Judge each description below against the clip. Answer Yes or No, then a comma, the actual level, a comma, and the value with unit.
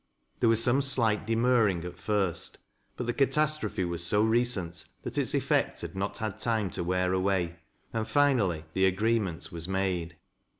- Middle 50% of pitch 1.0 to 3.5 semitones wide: No, average, 4.2 semitones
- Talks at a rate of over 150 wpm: Yes, average, 165 wpm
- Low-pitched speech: Yes, low, 100 Hz